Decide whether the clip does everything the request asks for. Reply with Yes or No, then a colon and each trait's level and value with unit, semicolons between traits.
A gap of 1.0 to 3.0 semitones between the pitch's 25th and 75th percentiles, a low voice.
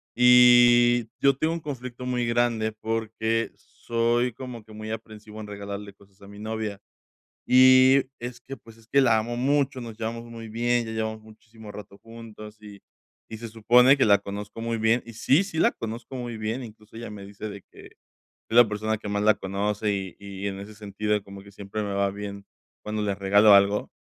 Yes: narrow, 2.6 semitones; low, 110 Hz